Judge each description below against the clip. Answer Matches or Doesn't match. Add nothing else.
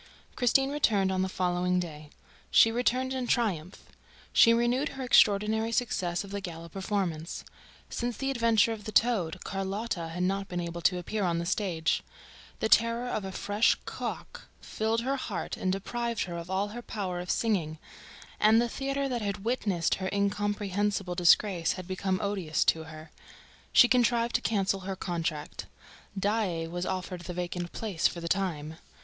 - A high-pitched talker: Matches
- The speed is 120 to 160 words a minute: Doesn't match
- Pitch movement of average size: Matches